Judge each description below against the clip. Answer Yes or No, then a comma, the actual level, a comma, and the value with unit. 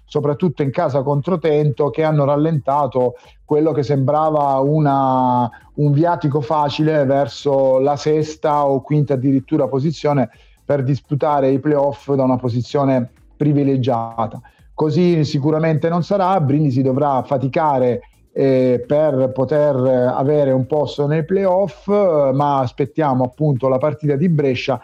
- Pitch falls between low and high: Yes, medium, 145 Hz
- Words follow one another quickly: No, average, 130 wpm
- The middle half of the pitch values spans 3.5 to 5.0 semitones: No, narrow, 2.4 semitones